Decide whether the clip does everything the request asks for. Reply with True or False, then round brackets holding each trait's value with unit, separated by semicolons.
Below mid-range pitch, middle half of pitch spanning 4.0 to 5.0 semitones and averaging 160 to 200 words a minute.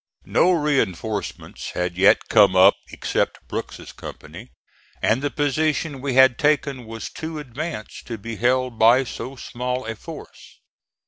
False (125 Hz; 4.5 semitones; 140 wpm)